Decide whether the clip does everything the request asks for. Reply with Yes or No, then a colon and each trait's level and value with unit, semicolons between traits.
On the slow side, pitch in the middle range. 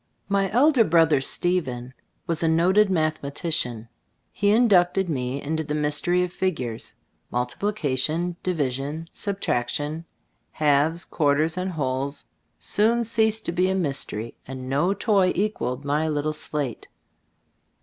Yes: slow, 120 wpm; medium, 160 Hz